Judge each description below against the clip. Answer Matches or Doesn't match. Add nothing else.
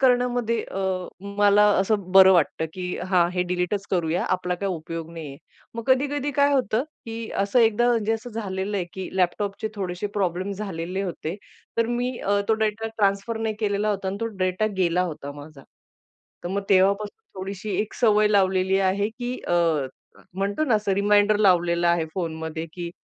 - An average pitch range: Matches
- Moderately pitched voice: Doesn't match